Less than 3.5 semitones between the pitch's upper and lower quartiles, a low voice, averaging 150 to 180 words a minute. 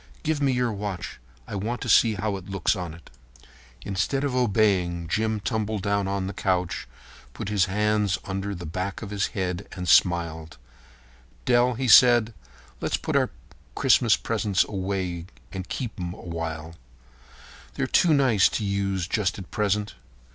Yes: average, 3.0 semitones; low, 100 Hz; average, 165 wpm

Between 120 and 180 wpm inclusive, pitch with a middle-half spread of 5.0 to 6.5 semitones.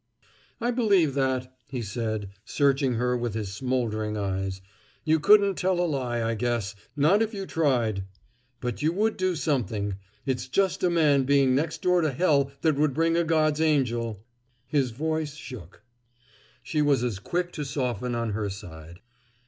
Yes: average, 170 wpm; wide, 5.5 semitones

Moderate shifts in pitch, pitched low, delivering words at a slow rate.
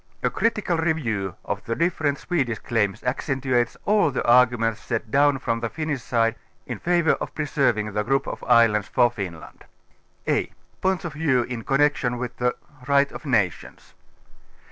No: average, 4.2 semitones; low, 125 Hz; average, 165 wpm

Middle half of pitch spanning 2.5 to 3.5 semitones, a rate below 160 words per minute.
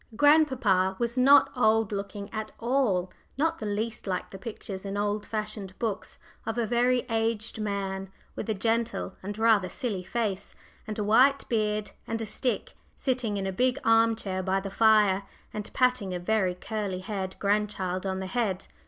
No: average, 3.0 semitones; average, 175 wpm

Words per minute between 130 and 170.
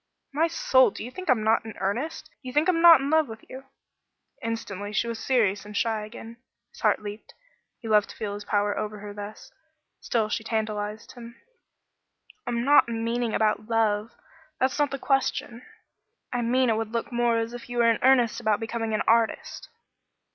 No: average, 200 wpm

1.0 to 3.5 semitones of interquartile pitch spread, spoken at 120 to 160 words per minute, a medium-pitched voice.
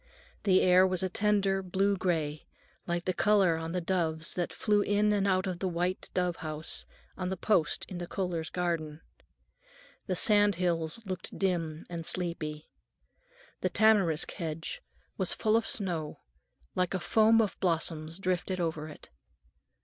Yes: average, 2.8 semitones; average, 155 wpm; medium, 180 Hz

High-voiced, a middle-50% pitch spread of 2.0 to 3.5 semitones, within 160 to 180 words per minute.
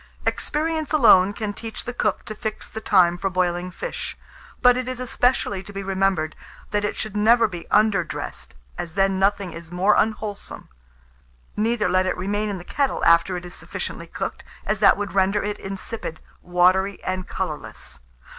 Yes: high, 200 Hz; average, 2.9 semitones; average, 175 wpm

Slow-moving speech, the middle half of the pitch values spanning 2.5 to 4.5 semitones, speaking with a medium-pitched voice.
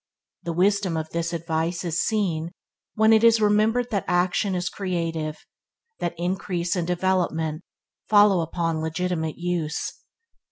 Yes: slow, 130 wpm; average, 2.9 semitones; medium, 175 Hz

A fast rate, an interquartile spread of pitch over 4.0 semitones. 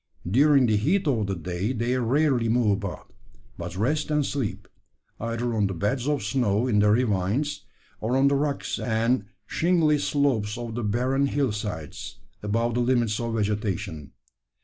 No: average, 165 wpm; average, 4.7 semitones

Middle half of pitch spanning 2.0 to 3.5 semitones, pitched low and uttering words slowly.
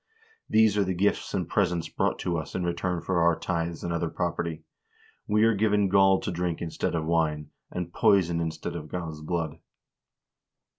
No: narrow, 2.4 semitones; very low, 85 Hz; average, 180 wpm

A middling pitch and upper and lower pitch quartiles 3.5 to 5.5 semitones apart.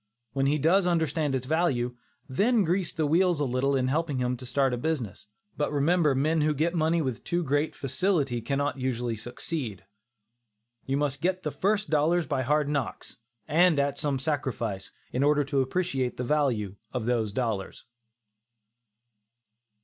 Yes: medium, 145 Hz; average, 4.0 semitones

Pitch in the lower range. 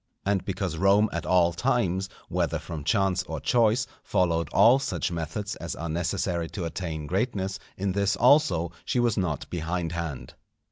Yes: very low, 90 Hz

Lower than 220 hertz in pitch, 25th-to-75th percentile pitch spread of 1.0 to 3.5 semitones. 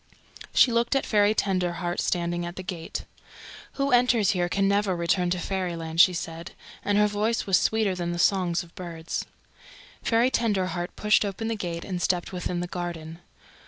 Yes: medium, 185 Hz; average, 3.1 semitones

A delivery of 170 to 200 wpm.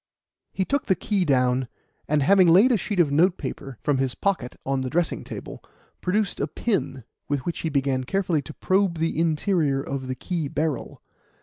Yes: average, 185 wpm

